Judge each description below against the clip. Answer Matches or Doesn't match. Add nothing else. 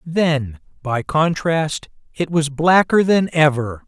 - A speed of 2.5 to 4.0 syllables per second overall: Matches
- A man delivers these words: Matches